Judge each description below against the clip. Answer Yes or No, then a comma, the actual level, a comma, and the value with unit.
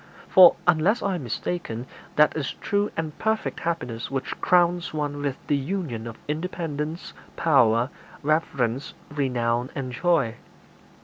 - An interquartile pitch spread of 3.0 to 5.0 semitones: No, wide, 5.4 semitones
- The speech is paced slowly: Yes, slow, 130 wpm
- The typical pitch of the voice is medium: Yes, medium, 150 Hz